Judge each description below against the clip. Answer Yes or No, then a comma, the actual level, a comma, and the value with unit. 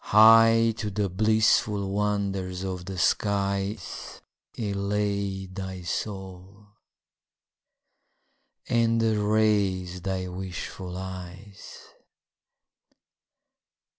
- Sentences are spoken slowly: Yes, slow, 70 wpm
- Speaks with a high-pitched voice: No, low, 100 Hz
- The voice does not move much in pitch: Yes, narrow, 2.0 semitones